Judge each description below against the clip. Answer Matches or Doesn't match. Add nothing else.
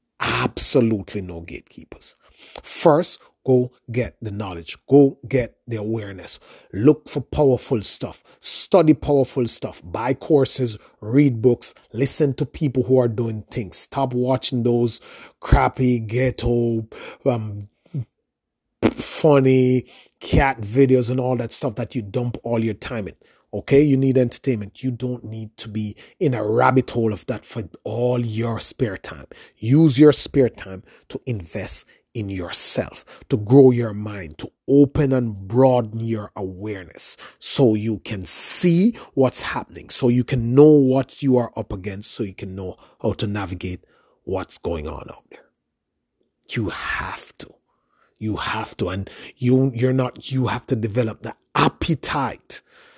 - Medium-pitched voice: Doesn't match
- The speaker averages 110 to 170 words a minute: Matches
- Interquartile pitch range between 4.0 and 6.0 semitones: Doesn't match